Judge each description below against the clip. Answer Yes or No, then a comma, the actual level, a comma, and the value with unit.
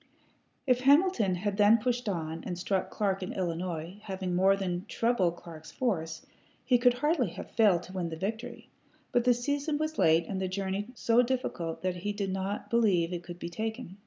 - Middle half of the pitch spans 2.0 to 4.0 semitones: No, average, 5.1 semitones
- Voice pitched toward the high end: Yes, high, 195 Hz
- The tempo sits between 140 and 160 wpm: No, average, 190 wpm